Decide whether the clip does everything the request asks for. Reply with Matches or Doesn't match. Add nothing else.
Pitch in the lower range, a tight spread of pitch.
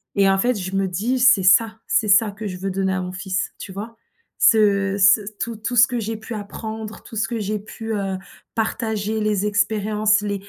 Doesn't match